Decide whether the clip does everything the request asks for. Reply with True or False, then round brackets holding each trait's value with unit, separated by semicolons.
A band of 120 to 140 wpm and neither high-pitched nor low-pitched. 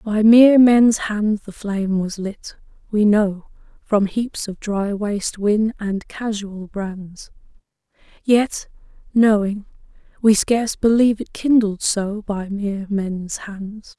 False (135 wpm; 210 Hz)